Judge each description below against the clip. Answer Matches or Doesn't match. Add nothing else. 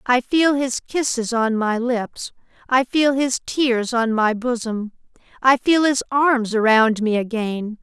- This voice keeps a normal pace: Matches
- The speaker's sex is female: Matches